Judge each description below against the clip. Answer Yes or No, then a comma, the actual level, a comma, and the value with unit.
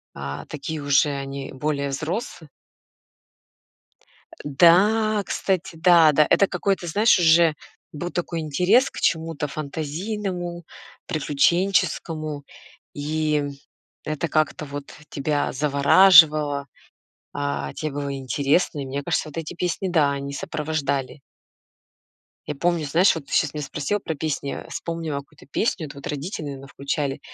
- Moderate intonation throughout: Yes, average, 3.4 semitones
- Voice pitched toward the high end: No, medium, 155 Hz